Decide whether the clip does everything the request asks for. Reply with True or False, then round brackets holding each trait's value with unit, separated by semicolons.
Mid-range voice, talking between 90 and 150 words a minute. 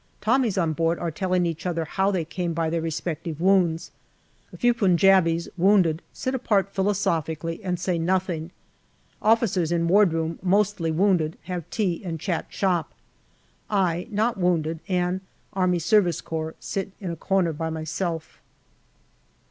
True (175 Hz; 140 wpm)